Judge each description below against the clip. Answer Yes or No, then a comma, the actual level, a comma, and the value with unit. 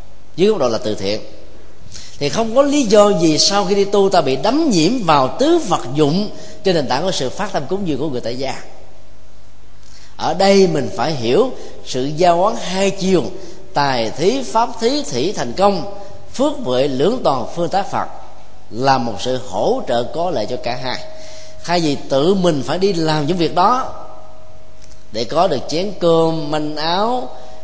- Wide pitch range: Yes, wide, 7.8 semitones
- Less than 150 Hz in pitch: No, medium, 155 Hz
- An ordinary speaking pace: Yes, average, 190 wpm